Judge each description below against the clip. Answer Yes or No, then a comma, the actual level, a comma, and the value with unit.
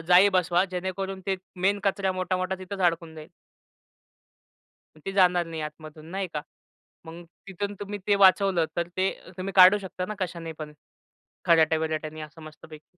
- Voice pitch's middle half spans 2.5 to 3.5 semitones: Yes, average, 3.0 semitones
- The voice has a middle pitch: Yes, medium, 180 Hz